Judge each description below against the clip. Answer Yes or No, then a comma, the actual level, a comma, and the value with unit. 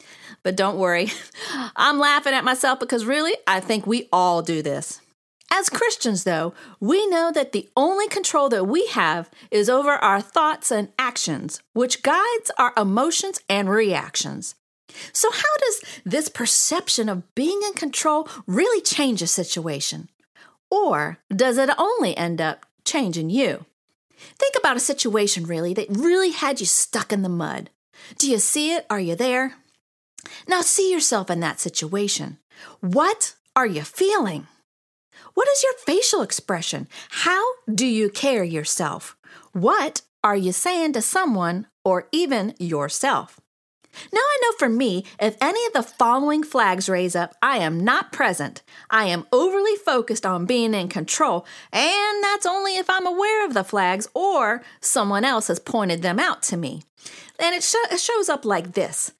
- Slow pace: No, average, 160 wpm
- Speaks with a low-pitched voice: No, very high, 255 Hz